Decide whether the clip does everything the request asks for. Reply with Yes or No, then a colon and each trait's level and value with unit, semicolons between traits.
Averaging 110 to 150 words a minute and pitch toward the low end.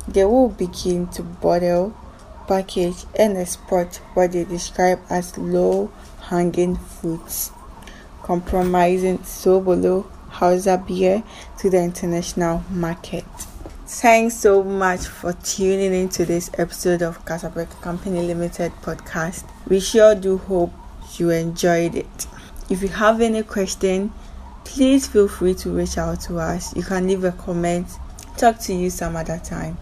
No: slow, 135 wpm; medium, 180 Hz